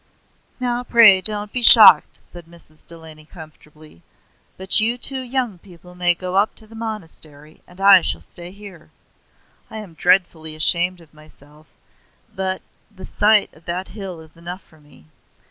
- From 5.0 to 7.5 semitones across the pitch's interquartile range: No, average, 4.6 semitones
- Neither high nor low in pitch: Yes, medium, 180 Hz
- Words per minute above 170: No, average, 160 wpm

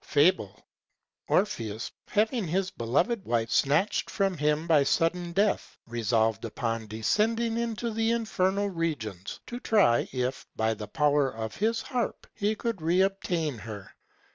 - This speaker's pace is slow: Yes, slow, 130 wpm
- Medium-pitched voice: Yes, medium, 165 Hz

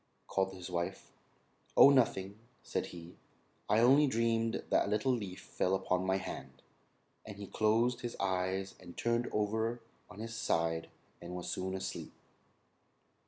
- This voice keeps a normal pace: Yes, average, 150 wpm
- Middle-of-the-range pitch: No, low, 100 Hz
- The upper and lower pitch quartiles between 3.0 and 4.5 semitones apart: Yes, average, 3.7 semitones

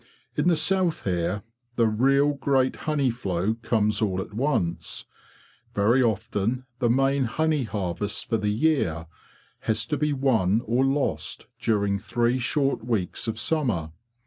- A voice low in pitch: Yes, low, 115 Hz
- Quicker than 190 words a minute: No, average, 145 wpm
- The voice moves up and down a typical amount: Yes, average, 4.9 semitones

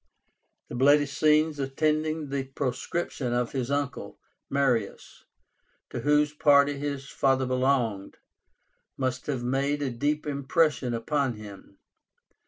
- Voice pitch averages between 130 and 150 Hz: Yes, medium, 140 Hz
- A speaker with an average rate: No, slow, 115 wpm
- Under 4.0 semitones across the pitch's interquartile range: Yes, narrow, 2.5 semitones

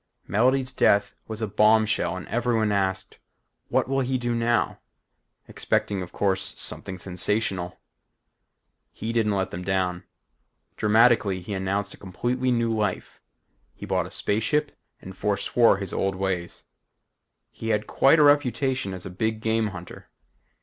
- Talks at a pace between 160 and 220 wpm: No, average, 145 wpm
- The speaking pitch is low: Yes, low, 105 Hz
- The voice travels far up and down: No, average, 3.6 semitones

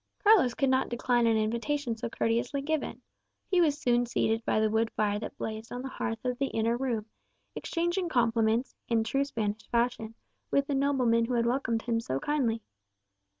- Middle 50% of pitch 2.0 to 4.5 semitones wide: Yes, average, 3.3 semitones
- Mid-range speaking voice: No, high, 235 Hz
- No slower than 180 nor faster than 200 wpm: Yes, average, 185 wpm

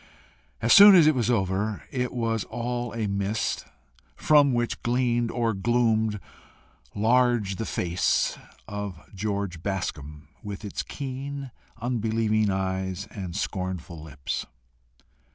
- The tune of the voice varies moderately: Yes, average, 4.0 semitones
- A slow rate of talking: Yes, slow, 115 wpm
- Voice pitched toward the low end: Yes, low, 110 Hz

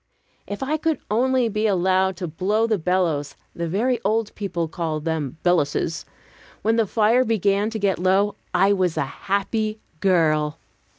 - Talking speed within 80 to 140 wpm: No, average, 160 wpm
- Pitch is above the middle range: Yes, high, 195 Hz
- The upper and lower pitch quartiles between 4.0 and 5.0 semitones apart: Yes, average, 4.3 semitones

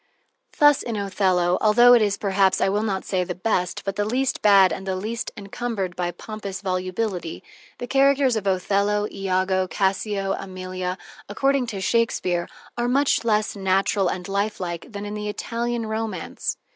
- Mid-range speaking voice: No, high, 200 Hz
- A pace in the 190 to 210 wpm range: No, average, 160 wpm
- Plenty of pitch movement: No, average, 3.0 semitones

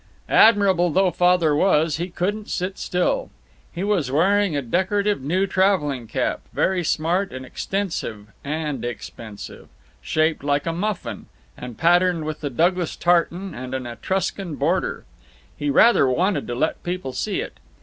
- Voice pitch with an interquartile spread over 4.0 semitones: Yes, average, 4.9 semitones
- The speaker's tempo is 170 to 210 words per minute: No, average, 150 wpm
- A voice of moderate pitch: Yes, medium, 170 Hz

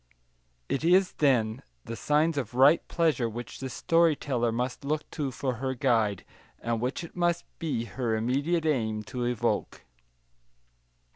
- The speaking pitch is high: No, low, 130 Hz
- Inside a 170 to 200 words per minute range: No, average, 150 wpm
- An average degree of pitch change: Yes, average, 4.6 semitones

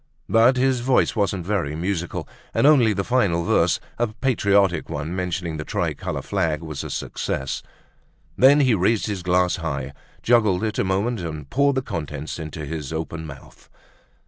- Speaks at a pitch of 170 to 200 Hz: No, very low, 90 Hz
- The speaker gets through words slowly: No, average, 165 wpm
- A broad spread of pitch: Yes, wide, 6.2 semitones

